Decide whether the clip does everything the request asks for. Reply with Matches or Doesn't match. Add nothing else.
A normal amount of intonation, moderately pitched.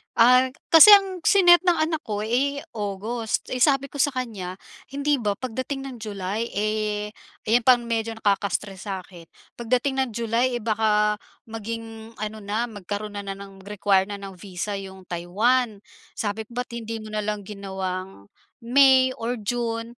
Doesn't match